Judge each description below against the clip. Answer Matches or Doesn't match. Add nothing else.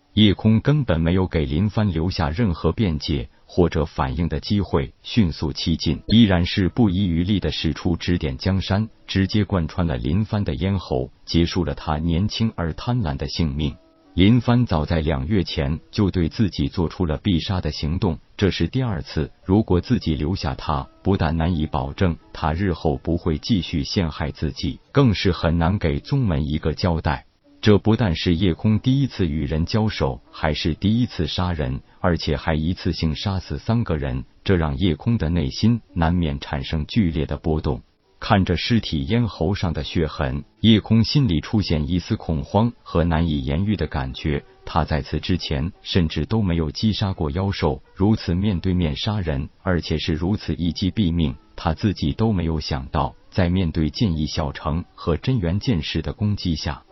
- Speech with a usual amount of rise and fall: Matches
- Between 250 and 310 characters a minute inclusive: Matches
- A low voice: Matches